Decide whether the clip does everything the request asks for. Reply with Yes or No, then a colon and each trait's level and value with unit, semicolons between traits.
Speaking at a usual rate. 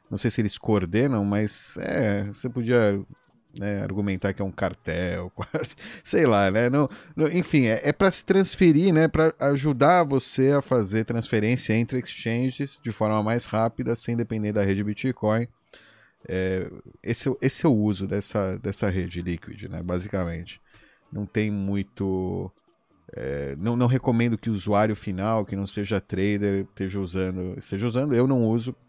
Yes: average, 165 wpm